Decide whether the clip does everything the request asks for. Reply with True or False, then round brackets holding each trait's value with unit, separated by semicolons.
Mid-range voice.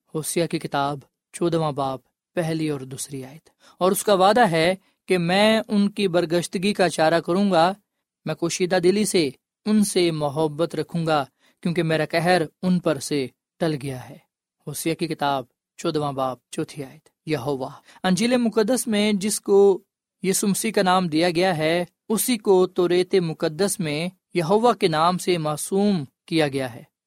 True (175 Hz)